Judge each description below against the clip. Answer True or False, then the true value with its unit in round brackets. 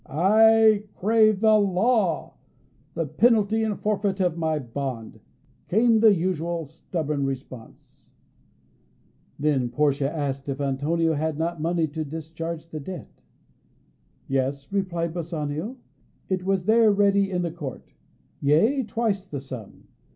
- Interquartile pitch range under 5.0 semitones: False (5.6 semitones)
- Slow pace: True (125 wpm)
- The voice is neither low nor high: True (170 Hz)